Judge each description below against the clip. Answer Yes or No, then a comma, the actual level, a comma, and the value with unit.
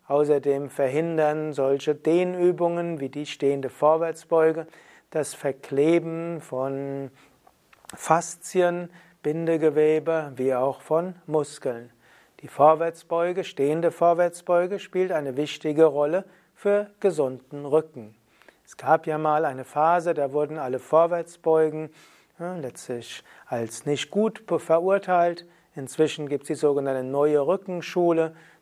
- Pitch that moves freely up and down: No, average, 3.1 semitones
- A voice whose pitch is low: No, medium, 155 Hz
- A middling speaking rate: No, slow, 105 wpm